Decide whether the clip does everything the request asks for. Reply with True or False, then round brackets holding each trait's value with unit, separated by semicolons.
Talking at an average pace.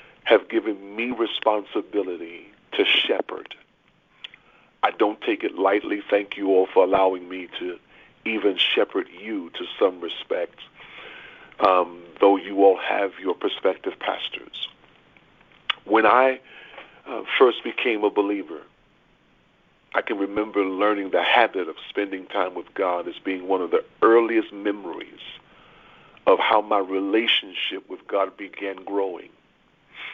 False (130 wpm)